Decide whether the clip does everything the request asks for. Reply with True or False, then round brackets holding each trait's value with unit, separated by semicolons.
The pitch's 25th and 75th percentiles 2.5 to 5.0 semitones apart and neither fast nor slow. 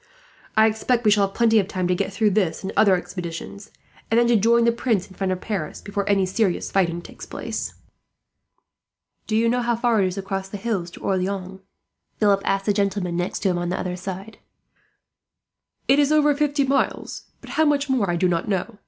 False (3.7 semitones; 215 wpm)